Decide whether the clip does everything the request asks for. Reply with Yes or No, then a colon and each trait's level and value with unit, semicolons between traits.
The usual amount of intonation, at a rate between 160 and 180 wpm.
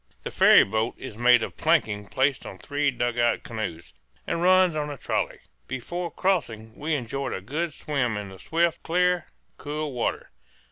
No: wide, 6.2 semitones; average, 170 wpm